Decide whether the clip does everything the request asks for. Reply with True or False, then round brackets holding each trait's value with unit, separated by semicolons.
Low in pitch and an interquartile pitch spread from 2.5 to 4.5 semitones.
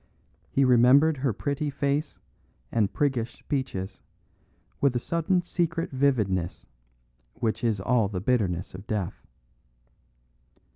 False (125 Hz; 5.4 semitones)